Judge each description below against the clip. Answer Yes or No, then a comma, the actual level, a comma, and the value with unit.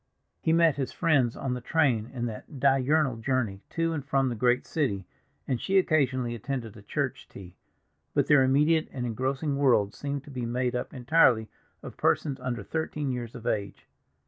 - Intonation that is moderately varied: Yes, average, 3.3 semitones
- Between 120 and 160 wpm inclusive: No, average, 180 wpm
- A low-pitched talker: Yes, low, 130 Hz